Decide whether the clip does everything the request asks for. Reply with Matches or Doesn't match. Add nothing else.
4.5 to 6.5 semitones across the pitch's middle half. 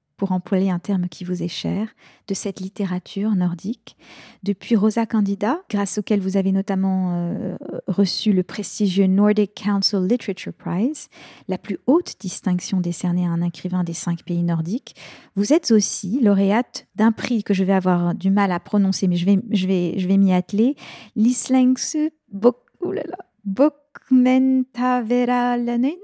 Doesn't match